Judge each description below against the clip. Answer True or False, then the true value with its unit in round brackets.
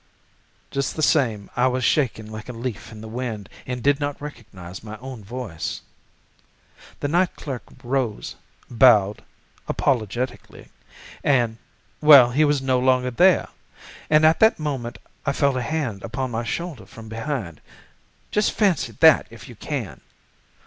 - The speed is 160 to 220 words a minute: False (150 wpm)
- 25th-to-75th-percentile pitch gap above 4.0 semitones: True (4.4 semitones)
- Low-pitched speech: True (125 Hz)